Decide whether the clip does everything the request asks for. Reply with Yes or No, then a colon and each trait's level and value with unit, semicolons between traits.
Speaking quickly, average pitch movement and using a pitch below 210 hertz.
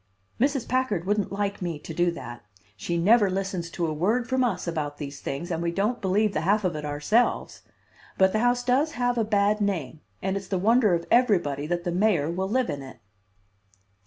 Yes: fast, 210 wpm; average, 4.6 semitones; high, 190 Hz